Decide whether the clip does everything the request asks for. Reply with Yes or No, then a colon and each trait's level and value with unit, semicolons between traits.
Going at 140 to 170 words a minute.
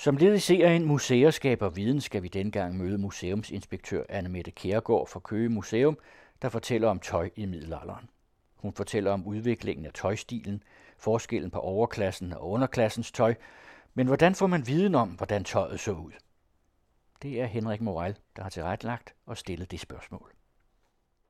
Yes: average, 160 wpm